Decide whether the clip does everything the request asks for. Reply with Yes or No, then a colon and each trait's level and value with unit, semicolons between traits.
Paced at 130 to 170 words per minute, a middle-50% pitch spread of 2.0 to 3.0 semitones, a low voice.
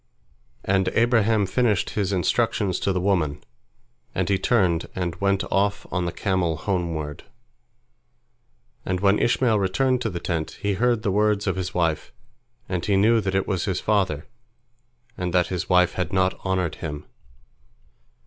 Yes: average, 160 wpm; narrow, 2.4 semitones; very low, 95 Hz